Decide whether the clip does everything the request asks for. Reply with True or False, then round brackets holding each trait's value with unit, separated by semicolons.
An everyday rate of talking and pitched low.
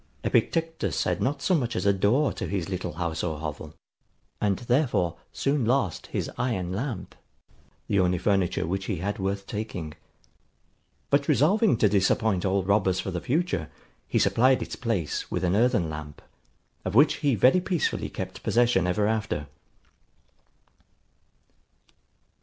True (145 wpm; 100 Hz)